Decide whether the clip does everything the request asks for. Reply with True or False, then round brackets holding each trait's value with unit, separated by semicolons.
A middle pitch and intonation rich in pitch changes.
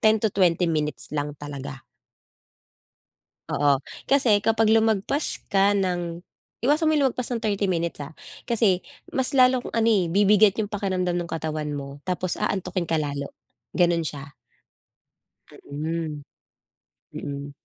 True (180 Hz; 6.2 semitones)